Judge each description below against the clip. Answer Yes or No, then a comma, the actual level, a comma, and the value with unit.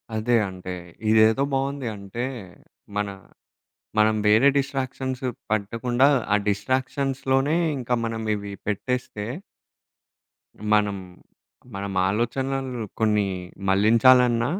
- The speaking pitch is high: No, low, 115 Hz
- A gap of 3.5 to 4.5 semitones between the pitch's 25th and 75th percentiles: Yes, average, 3.8 semitones